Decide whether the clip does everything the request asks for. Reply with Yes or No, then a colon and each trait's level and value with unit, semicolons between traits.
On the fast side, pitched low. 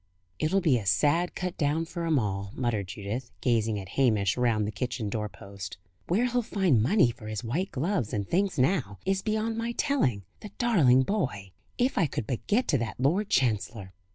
No: average, 195 wpm; low, 130 Hz